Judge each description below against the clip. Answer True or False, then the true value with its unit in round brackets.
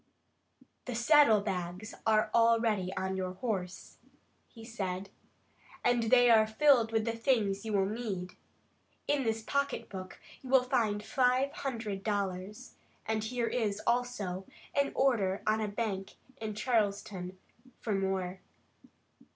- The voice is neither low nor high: False (215 Hz)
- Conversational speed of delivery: False (130 wpm)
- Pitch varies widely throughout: False (3.6 semitones)